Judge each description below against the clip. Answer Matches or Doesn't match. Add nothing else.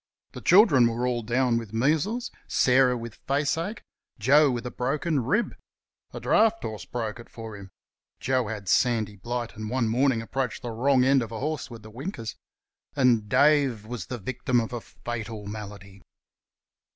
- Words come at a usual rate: Matches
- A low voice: Matches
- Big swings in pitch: Doesn't match